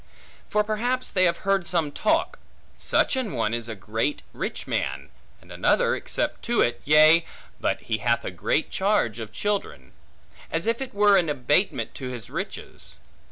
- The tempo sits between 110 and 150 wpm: No, average, 170 wpm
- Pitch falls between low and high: Yes, medium, 155 Hz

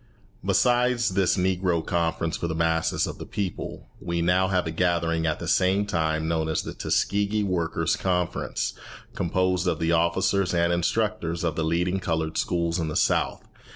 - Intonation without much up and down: Yes, narrow, 2.3 semitones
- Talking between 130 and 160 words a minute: No, average, 170 wpm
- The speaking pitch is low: Yes, very low, 85 Hz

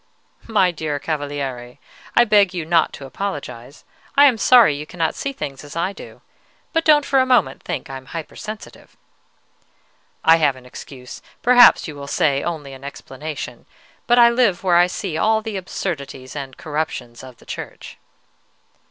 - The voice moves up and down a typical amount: No, wide, 7.1 semitones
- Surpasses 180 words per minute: No, average, 170 wpm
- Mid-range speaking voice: Yes, medium, 160 Hz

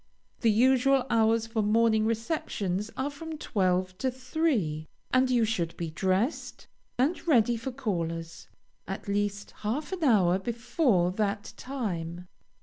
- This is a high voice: Yes, high, 220 Hz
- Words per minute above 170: No, slow, 135 wpm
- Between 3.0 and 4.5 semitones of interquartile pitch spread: No, wide, 5.4 semitones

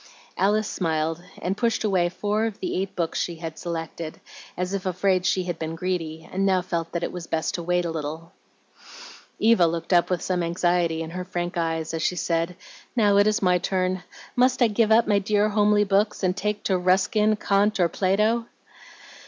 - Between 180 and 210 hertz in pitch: Yes, medium, 185 Hz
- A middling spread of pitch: Yes, average, 3.4 semitones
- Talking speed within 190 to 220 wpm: Yes, average, 200 wpm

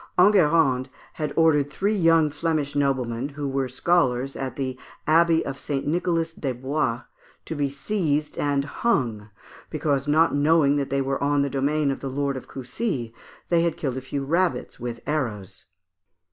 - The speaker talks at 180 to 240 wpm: No, average, 165 wpm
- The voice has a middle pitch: Yes, medium, 145 Hz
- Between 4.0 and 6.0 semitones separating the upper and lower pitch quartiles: No, average, 3.3 semitones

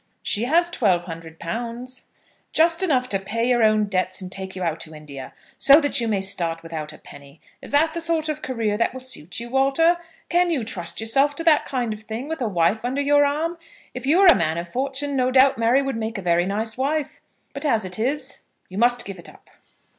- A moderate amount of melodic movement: No, wide, 7.0 semitones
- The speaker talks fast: Yes, fast, 230 wpm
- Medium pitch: No, high, 235 Hz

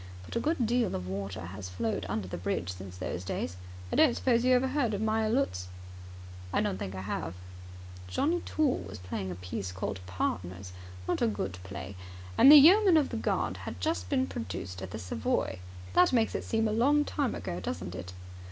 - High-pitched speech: No, low, 100 Hz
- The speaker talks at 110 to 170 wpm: No, fast, 205 wpm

